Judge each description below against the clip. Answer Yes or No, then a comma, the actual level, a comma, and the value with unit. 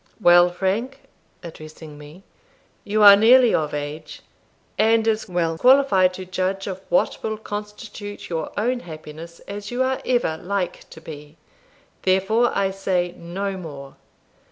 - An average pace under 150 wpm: Yes, average, 140 wpm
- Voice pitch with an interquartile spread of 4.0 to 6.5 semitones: Yes, average, 4.7 semitones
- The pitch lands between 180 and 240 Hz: Yes, high, 190 Hz